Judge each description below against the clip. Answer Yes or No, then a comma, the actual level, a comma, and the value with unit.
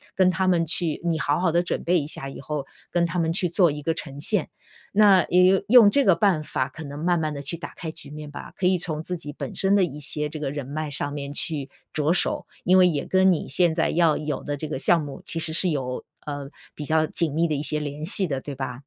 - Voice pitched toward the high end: No, medium, 160 Hz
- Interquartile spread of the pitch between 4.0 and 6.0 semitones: No, average, 3.4 semitones